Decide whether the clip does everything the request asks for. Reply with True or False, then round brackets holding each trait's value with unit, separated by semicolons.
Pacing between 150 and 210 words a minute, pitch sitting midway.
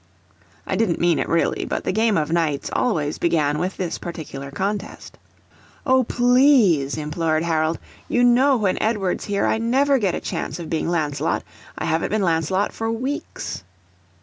True (165 wpm; 180 Hz)